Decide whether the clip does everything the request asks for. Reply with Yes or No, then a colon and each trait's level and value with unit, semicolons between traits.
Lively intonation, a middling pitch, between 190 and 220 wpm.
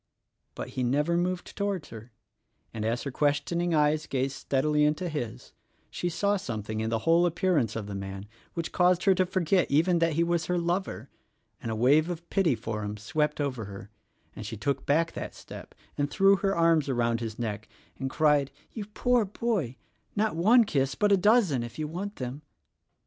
Yes: wide, 6.7 semitones; medium, 150 Hz; average, 200 wpm